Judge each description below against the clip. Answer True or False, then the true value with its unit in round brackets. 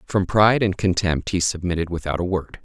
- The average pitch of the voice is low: True (90 Hz)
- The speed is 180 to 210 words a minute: True (205 wpm)